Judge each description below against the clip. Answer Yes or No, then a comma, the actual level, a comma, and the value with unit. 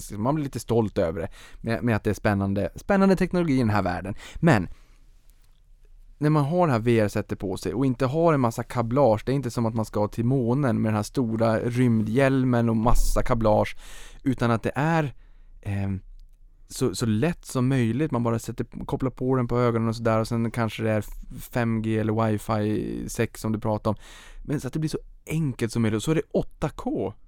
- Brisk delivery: Yes, fast, 215 wpm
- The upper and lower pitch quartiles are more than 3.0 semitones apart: Yes, average, 3.7 semitones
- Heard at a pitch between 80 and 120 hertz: Yes, low, 115 Hz